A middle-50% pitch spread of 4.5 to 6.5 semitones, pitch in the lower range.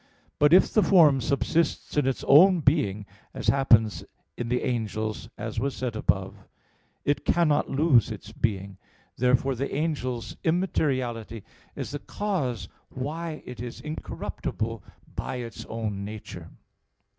Yes: average, 5.1 semitones; low, 125 Hz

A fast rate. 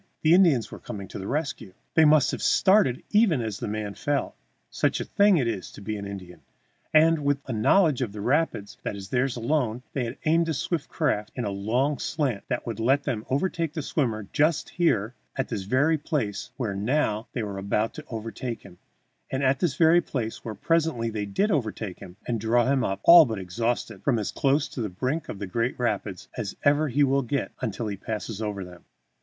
Yes: fast, 215 wpm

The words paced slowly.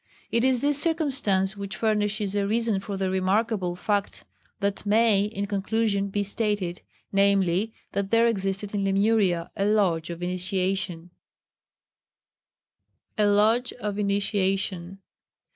Yes: slow, 125 wpm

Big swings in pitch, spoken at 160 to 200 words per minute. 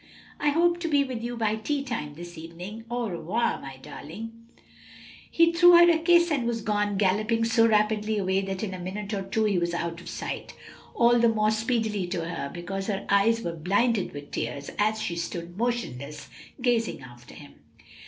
No: average, 5.0 semitones; average, 190 wpm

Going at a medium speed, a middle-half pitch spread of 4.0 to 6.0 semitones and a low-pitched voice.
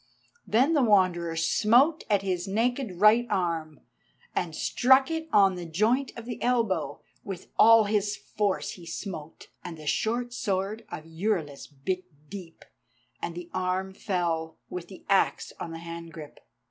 No: average, 155 wpm; average, 4.8 semitones; high, 190 Hz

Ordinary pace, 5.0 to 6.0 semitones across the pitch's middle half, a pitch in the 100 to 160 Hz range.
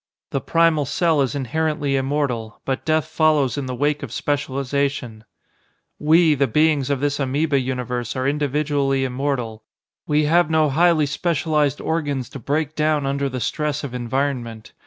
No: average, 155 wpm; narrow, 2.6 semitones; medium, 140 Hz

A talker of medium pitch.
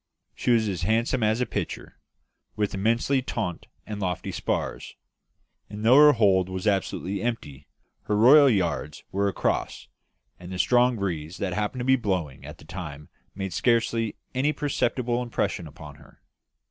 No: low, 105 Hz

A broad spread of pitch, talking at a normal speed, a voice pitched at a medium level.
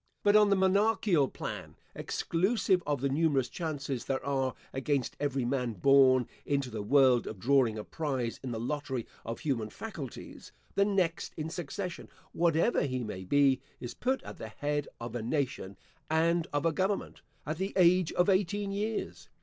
Yes: wide, 5.8 semitones; average, 170 wpm; medium, 145 Hz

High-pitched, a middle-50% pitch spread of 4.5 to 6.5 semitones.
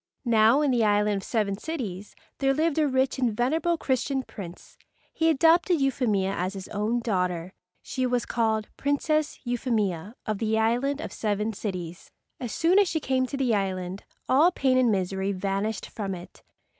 Yes: high, 230 Hz; wide, 5.4 semitones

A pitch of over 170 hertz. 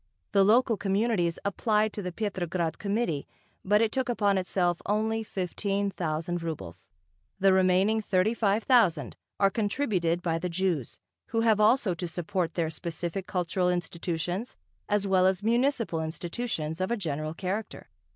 Yes: high, 190 Hz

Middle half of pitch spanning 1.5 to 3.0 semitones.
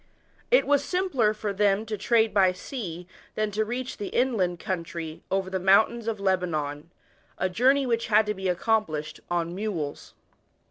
No: average, 4.0 semitones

